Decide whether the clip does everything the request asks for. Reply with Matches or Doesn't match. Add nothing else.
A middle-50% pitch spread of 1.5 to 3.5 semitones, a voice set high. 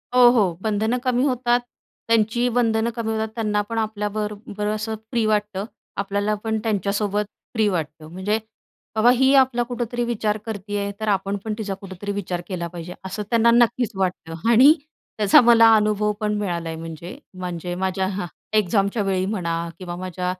Matches